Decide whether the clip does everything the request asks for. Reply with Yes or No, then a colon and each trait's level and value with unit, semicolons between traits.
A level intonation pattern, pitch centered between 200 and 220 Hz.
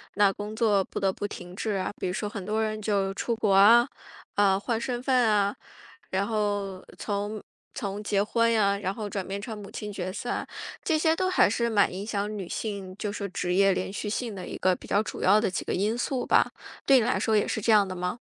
Yes: narrow, 2.0 semitones; high, 205 Hz